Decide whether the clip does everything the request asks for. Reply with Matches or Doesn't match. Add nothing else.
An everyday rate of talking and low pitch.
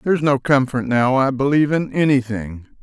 Matches